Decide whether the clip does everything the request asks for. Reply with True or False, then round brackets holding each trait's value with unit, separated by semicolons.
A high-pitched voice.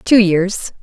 True (195 Hz)